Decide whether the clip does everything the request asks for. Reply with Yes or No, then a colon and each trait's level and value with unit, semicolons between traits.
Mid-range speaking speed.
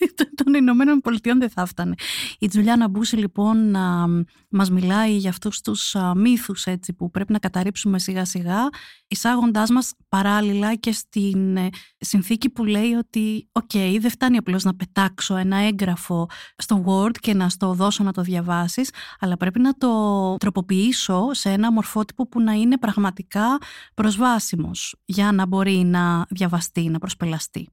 Yes: average, 150 wpm